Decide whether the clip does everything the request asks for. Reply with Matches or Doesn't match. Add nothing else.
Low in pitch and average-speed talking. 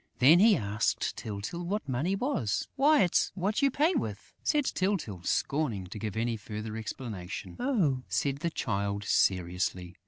Matches